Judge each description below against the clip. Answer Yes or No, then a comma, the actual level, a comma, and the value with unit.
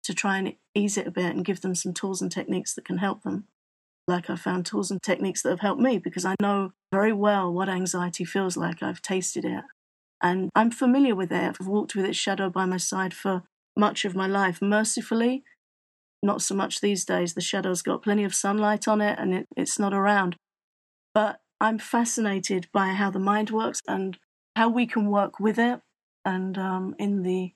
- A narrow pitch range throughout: Yes, narrow, 2.0 semitones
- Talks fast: Yes, fast, 210 wpm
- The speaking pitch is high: Yes, high, 195 Hz